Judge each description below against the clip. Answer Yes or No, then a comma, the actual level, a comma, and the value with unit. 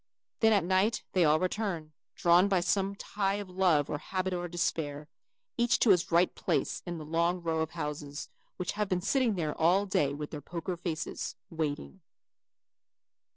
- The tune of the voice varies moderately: Yes, average, 3.4 semitones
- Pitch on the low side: No, medium, 175 Hz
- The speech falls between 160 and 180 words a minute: Yes, average, 175 wpm